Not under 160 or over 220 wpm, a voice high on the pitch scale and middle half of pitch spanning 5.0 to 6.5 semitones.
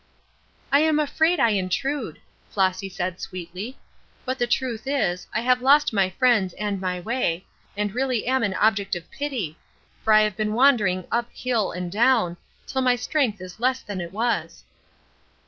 Yes: average, 170 wpm; high, 220 Hz; wide, 5.5 semitones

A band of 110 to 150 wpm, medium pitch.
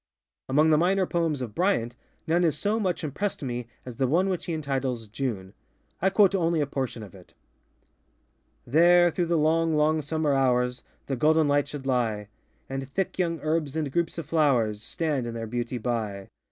No: average, 185 wpm; medium, 145 Hz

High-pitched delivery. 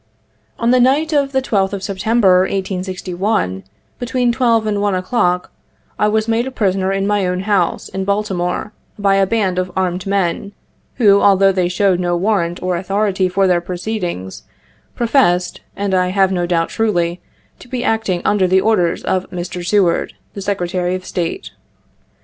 Yes: high, 195 Hz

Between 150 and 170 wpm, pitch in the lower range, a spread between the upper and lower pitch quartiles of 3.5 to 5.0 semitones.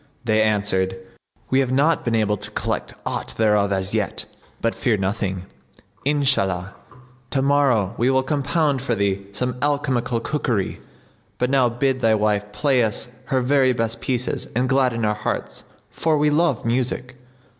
Yes: average, 155 wpm; low, 120 Hz; average, 4.3 semitones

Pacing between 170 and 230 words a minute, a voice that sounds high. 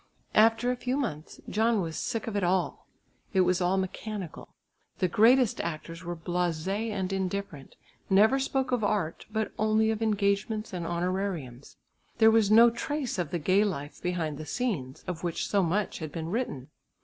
Yes: average, 175 wpm; high, 195 Hz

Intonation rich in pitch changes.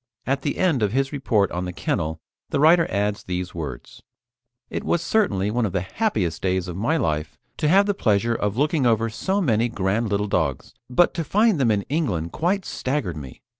Yes: wide, 8.3 semitones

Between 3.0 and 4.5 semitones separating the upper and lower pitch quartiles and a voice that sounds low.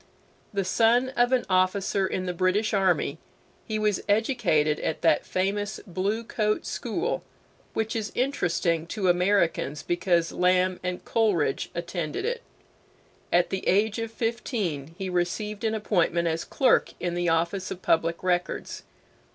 No: average, 3.8 semitones; medium, 185 Hz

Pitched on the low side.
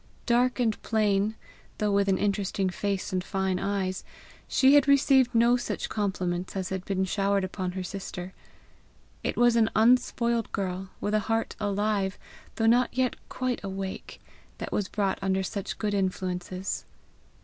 No: high, 200 Hz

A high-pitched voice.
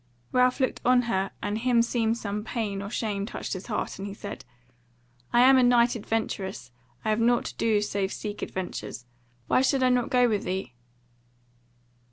Yes: high, 225 Hz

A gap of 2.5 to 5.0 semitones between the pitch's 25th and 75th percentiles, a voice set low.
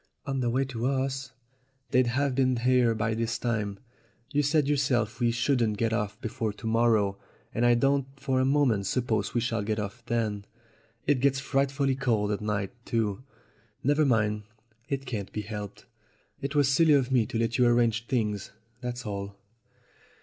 Yes: average, 3.7 semitones; low, 120 Hz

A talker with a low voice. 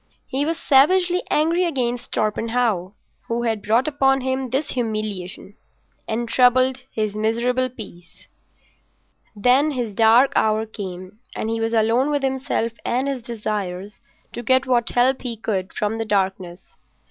No: high, 235 Hz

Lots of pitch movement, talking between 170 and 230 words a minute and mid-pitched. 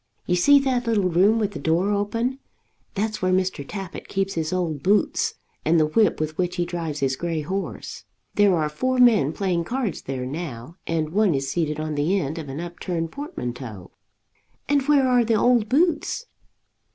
Yes: wide, 5.8 semitones; average, 185 wpm; medium, 180 Hz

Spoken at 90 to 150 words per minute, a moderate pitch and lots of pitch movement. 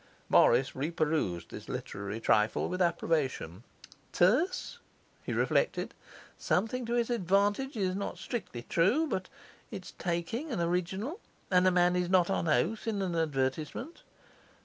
Yes: slow, 135 wpm; medium, 180 Hz; wide, 5.9 semitones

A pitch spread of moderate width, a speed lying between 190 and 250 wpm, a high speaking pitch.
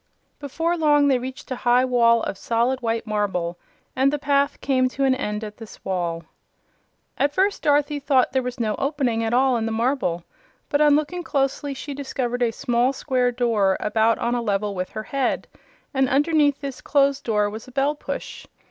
Yes: average, 3.8 semitones; average, 195 wpm; very high, 255 Hz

